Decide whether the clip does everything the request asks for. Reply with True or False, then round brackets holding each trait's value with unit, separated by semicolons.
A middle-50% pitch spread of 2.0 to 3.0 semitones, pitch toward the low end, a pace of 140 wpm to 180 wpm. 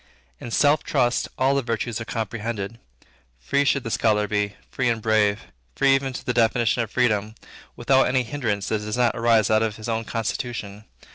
False (2.4 semitones; 115 Hz; 190 wpm)